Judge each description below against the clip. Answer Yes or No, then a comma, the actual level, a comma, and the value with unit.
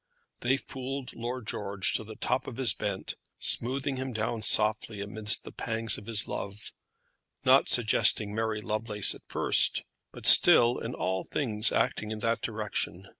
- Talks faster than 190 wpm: No, average, 160 wpm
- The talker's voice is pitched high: No, low, 110 Hz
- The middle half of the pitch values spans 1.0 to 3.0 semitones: Yes, narrow, 2.5 semitones